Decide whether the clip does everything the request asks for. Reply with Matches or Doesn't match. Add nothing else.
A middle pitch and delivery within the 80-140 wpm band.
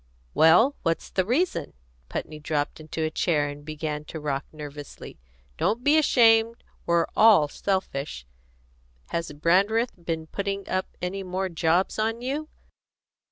Matches